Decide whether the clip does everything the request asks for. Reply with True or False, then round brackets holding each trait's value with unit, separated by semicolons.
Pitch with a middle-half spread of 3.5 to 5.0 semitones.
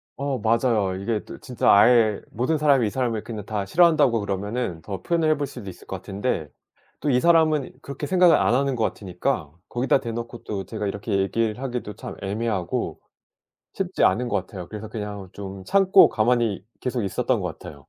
True (4.5 semitones)